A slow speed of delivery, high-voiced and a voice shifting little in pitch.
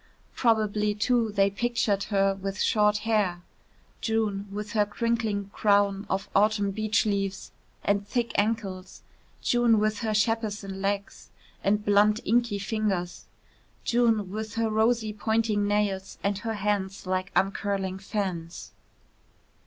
Yes: slow, 125 wpm; high, 210 Hz; narrow, 1.8 semitones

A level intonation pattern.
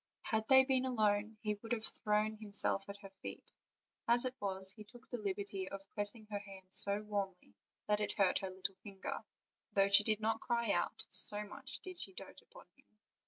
Yes: narrow, 2.3 semitones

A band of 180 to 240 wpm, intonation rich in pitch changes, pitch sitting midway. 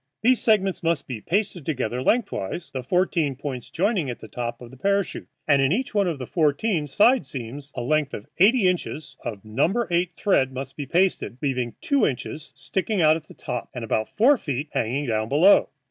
Yes: average, 200 wpm; wide, 6.8 semitones; medium, 150 Hz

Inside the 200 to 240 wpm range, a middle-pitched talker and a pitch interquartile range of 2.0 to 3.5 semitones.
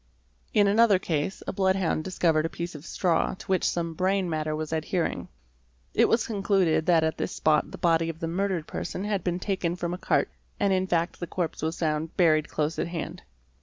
Yes: fast, 205 wpm; medium, 170 Hz; average, 2.8 semitones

